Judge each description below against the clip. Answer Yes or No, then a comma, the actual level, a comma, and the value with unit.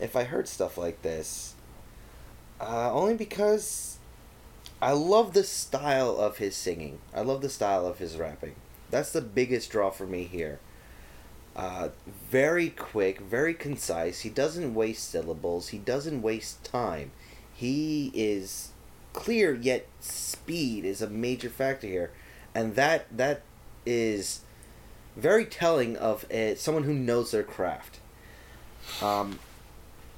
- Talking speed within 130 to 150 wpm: Yes, slow, 135 wpm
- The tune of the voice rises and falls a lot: Yes, wide, 6.8 semitones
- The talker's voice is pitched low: Yes, low, 120 Hz